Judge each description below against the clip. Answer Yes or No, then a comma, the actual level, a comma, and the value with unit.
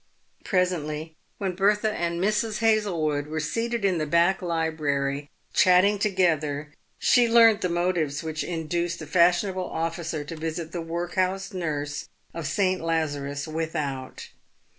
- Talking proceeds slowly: Yes, slow, 130 wpm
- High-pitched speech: No, medium, 170 Hz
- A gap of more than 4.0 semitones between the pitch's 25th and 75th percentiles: No, average, 3.4 semitones